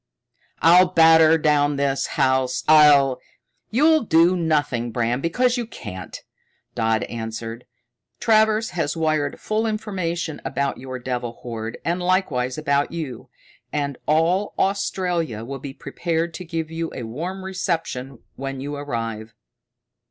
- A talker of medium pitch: Yes, medium, 150 Hz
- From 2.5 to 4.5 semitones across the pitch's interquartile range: No, wide, 5.5 semitones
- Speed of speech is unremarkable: No, slow, 130 wpm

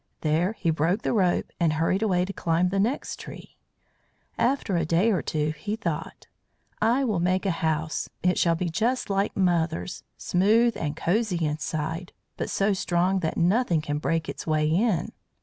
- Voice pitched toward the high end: No, medium, 180 Hz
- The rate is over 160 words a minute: Yes, average, 175 wpm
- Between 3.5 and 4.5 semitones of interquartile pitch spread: Yes, average, 3.8 semitones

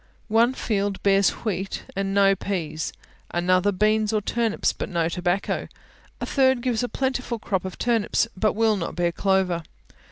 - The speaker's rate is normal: Yes, average, 160 wpm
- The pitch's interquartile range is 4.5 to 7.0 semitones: No, average, 3.4 semitones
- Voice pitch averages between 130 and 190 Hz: No, high, 200 Hz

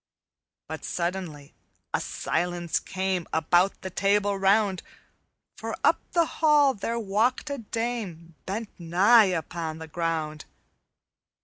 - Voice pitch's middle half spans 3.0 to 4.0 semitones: No, average, 4.6 semitones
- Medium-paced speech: No, slow, 115 wpm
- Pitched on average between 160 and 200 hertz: Yes, high, 190 Hz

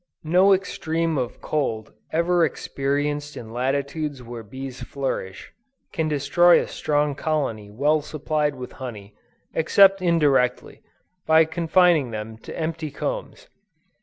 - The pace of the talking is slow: Yes, slow, 120 wpm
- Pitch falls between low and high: Yes, medium, 150 Hz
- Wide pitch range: No, average, 3.9 semitones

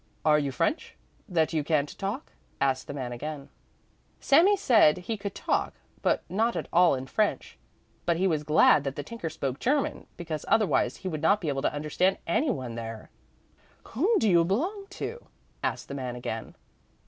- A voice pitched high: No, medium, 165 Hz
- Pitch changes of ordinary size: No, wide, 7.5 semitones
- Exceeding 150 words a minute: Yes, average, 185 wpm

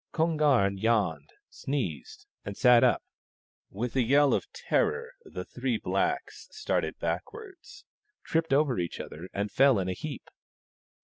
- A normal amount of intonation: No, wide, 7.6 semitones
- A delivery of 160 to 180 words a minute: No, average, 140 wpm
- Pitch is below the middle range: Yes, low, 125 Hz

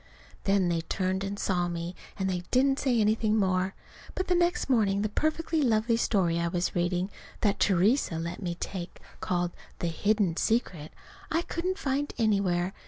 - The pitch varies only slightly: No, average, 4.8 semitones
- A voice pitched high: Yes, high, 195 Hz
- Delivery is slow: No, average, 170 wpm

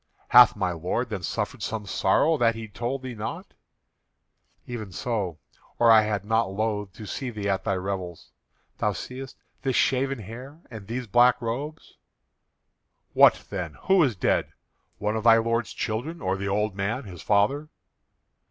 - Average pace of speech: Yes, average, 160 wpm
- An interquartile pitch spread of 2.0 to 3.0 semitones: No, average, 3.8 semitones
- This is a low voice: Yes, low, 110 Hz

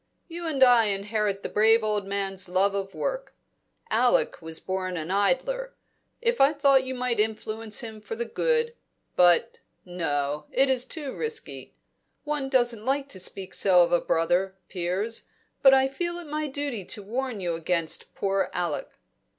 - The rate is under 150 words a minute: No, average, 165 wpm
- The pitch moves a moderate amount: No, wide, 6.2 semitones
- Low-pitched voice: No, high, 220 Hz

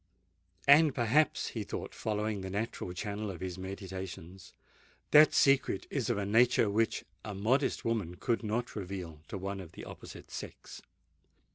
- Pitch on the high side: No, low, 105 Hz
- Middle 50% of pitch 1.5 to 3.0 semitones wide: No, average, 3.7 semitones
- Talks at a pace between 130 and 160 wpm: Yes, average, 155 wpm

